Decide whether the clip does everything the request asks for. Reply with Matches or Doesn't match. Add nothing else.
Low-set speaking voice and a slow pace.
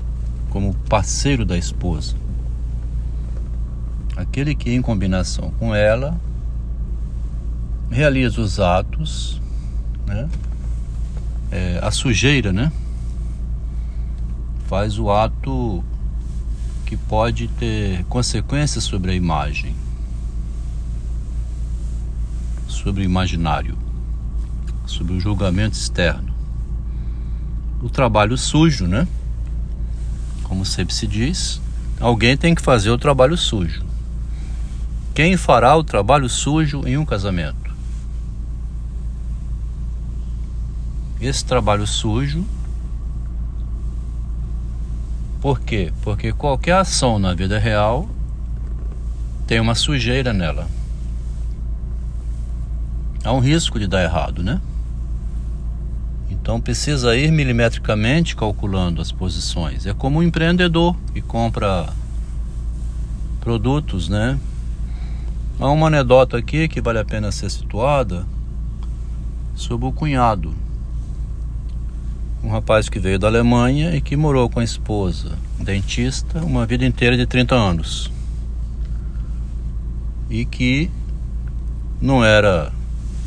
Matches